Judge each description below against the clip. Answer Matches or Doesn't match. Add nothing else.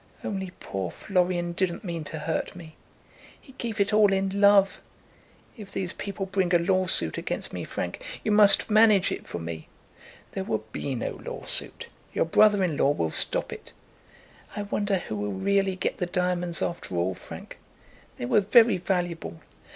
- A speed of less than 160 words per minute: Doesn't match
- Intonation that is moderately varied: Matches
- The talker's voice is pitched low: Doesn't match